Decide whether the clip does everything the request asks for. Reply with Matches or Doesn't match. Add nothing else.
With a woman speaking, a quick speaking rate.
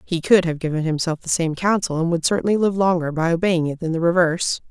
Matches